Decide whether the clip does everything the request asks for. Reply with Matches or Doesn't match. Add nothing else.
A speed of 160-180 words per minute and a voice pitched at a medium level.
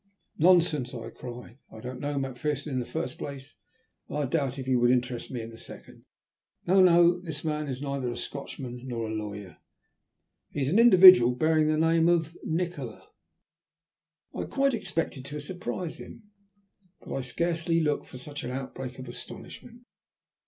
Matches